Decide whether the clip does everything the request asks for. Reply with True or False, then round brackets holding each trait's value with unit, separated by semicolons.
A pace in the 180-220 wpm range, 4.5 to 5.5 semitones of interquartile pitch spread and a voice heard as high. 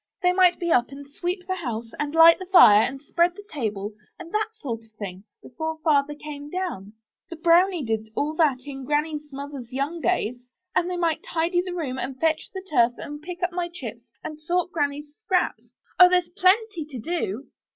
True (200 wpm; 5.0 semitones; 305 Hz)